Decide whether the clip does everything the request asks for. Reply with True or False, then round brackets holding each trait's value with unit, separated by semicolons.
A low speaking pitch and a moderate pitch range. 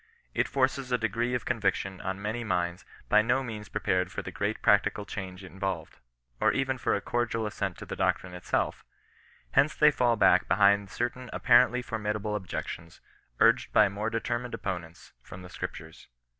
True (105 Hz; 4.2 semitones)